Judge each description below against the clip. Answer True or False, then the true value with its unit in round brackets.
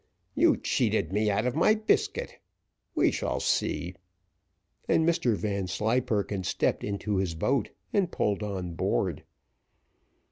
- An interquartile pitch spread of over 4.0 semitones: True (4.8 semitones)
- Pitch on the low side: True (105 Hz)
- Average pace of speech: False (120 wpm)